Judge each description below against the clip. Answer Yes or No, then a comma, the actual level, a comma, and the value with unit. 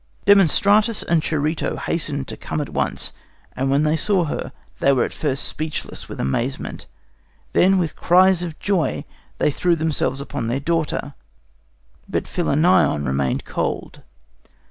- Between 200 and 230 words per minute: No, average, 145 wpm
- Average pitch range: Yes, average, 4.2 semitones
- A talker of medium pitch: Yes, medium, 155 Hz